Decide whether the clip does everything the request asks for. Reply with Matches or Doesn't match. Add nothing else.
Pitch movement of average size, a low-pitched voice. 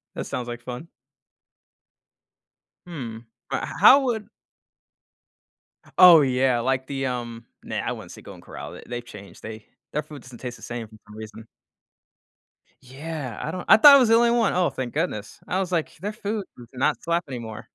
Doesn't match